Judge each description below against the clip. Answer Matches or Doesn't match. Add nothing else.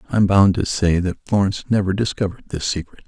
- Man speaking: Matches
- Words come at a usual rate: Doesn't match